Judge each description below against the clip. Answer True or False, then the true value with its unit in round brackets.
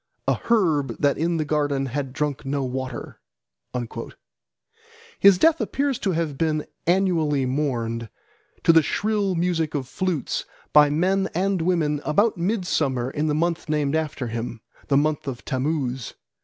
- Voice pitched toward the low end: False (150 Hz)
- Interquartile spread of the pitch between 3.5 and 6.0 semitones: True (4.4 semitones)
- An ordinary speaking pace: True (145 wpm)